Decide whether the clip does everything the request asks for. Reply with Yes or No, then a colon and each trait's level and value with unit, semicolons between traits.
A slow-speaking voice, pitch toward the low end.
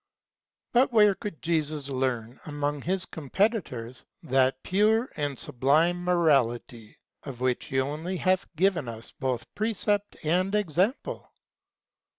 No: slow, 120 wpm; medium, 155 Hz